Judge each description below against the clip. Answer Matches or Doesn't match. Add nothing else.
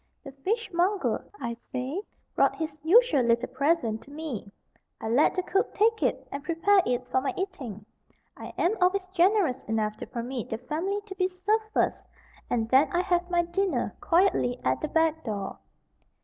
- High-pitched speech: Matches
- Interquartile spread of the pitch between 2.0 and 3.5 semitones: Doesn't match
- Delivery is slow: Doesn't match